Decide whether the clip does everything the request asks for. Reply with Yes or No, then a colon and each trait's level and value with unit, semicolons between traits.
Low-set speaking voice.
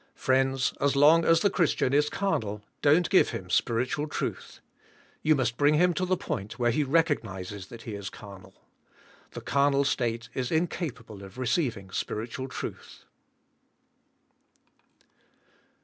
Yes: low, 130 Hz